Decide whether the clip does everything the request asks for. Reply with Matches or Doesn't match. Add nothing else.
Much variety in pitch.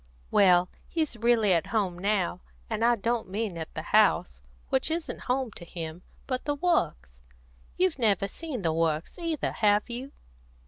Matches